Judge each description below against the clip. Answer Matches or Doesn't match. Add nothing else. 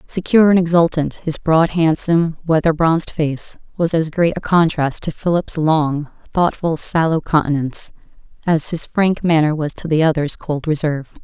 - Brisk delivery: Doesn't match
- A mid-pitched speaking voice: Matches